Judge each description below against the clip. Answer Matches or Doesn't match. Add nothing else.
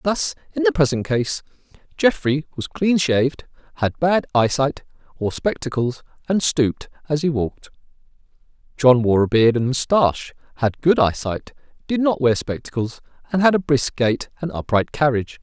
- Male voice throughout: Matches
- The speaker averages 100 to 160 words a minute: Matches